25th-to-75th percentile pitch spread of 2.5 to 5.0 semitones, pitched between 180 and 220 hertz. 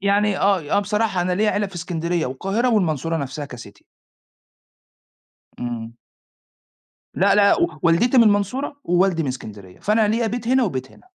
No: wide, 5.5 semitones; high, 190 Hz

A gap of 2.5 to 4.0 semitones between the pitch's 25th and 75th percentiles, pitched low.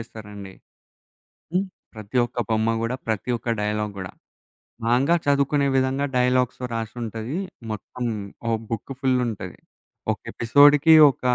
Yes: average, 3.4 semitones; low, 120 Hz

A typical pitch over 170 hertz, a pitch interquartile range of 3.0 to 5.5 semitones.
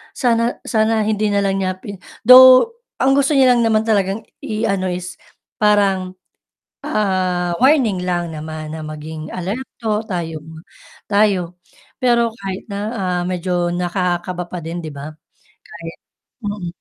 Yes: high, 190 Hz; average, 3.7 semitones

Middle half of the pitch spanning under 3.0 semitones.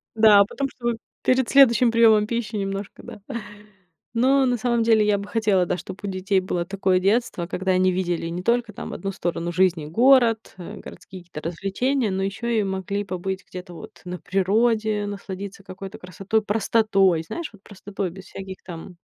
No: average, 3.3 semitones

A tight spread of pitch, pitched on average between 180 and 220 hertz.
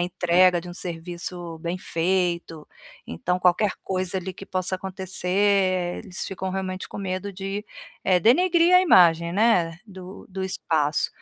Yes: narrow, 1.7 semitones; medium, 185 Hz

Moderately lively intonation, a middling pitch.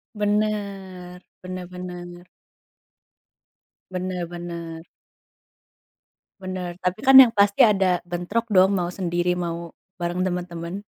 No: narrow, 2.1 semitones; medium, 180 Hz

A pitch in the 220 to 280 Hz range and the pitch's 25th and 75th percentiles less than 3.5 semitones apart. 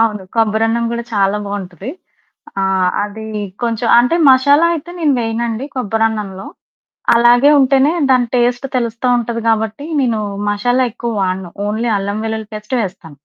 Yes: high, 225 Hz; average, 2.9 semitones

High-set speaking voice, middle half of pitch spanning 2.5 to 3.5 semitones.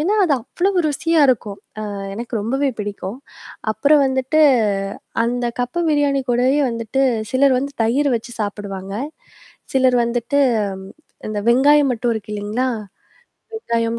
No: high, 245 Hz; average, 4.0 semitones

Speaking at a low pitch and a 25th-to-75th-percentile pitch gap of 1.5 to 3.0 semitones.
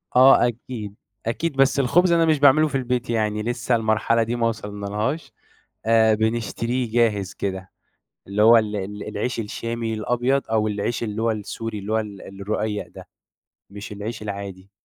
Yes: low, 110 Hz; average, 2.7 semitones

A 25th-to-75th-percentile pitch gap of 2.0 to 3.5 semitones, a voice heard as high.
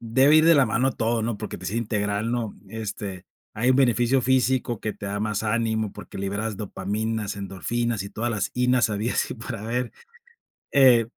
No: average, 2.8 semitones; low, 115 Hz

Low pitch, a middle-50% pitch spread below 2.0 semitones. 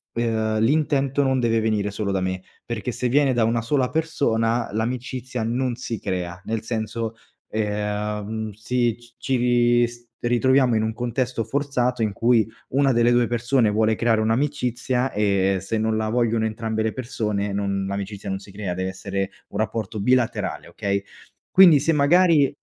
No: low, 115 Hz; average, 2.9 semitones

